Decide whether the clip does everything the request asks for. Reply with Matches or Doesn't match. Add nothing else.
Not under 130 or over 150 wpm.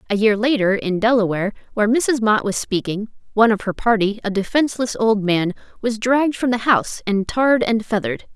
Doesn't match